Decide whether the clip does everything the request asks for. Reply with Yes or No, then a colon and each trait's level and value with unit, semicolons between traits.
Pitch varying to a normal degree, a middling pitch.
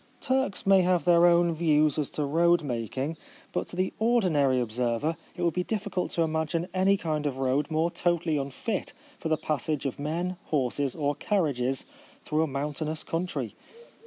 Yes: average, 3.5 semitones; medium, 160 Hz